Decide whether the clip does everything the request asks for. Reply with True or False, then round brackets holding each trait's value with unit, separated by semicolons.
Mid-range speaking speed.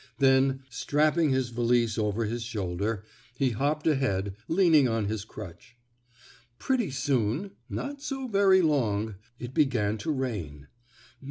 False (125 wpm)